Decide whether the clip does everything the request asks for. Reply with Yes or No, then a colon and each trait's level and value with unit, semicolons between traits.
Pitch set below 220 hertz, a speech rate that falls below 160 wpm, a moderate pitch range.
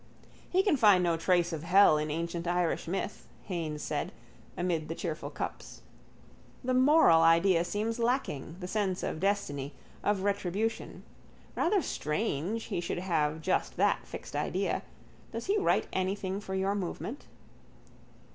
Yes: medium, 185 Hz; average, 145 wpm; average, 4.0 semitones